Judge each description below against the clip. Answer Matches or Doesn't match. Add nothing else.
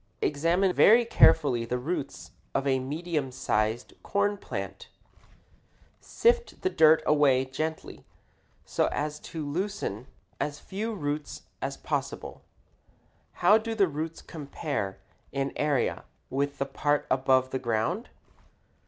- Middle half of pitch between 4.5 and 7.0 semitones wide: Matches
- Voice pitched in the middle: Matches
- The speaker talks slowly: Matches